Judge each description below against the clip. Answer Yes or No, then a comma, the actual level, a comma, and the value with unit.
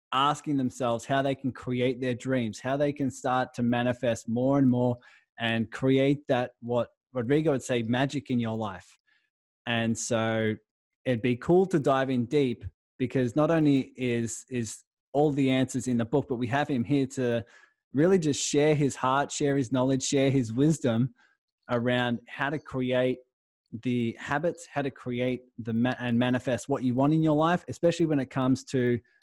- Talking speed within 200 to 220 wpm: No, average, 185 wpm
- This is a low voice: Yes, low, 130 Hz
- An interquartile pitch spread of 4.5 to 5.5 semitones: No, narrow, 2.5 semitones